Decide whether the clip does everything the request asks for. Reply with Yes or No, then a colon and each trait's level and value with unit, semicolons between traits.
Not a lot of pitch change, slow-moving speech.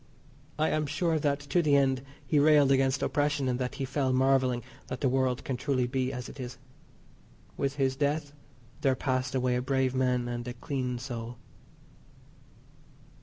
No: narrow, 2.0 semitones; average, 170 wpm